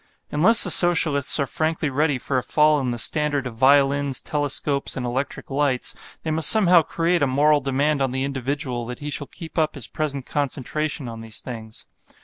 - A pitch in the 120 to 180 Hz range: Yes, medium, 140 Hz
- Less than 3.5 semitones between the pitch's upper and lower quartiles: Yes, average, 2.7 semitones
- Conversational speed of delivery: Yes, average, 190 wpm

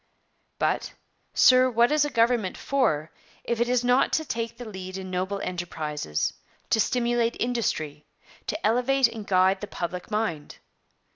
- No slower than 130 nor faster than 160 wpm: Yes, average, 150 wpm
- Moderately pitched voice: No, high, 225 Hz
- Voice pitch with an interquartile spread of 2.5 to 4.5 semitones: No, average, 5.0 semitones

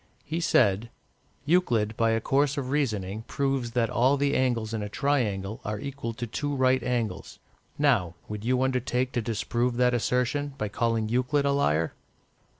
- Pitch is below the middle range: Yes, low, 125 Hz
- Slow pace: No, average, 165 wpm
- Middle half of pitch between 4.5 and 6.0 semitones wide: No, average, 3.9 semitones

